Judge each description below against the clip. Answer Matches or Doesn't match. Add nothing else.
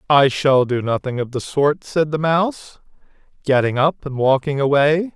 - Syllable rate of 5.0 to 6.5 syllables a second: Doesn't match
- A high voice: Doesn't match